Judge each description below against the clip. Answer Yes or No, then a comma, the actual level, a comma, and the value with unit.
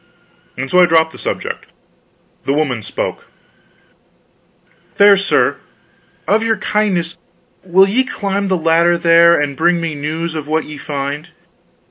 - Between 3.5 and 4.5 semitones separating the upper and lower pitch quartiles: Yes, average, 3.9 semitones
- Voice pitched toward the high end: No, medium, 170 Hz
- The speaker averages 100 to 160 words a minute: Yes, average, 140 wpm